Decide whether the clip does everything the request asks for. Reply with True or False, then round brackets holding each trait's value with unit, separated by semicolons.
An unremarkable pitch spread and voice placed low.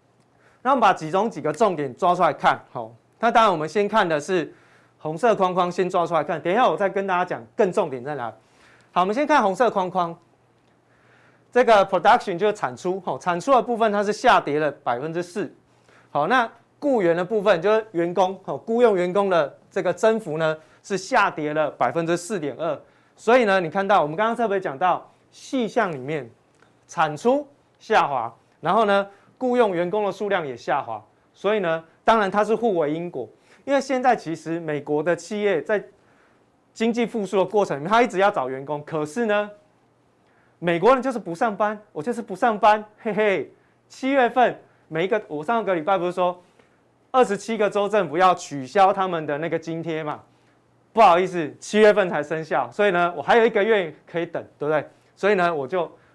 False (4.6 semitones; 190 Hz)